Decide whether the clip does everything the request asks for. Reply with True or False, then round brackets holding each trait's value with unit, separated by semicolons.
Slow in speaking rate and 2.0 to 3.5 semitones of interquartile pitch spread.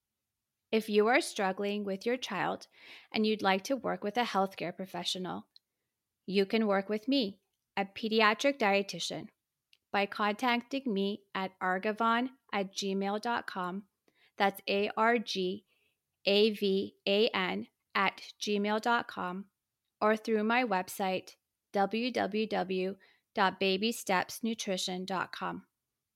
True (105 wpm; 2.6 semitones)